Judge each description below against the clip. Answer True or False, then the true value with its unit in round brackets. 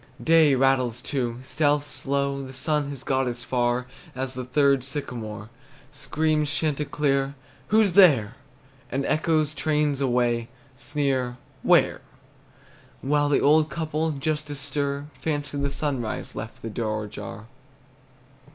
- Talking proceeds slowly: True (125 wpm)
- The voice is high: False (140 Hz)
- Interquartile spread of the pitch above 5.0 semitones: False (2.9 semitones)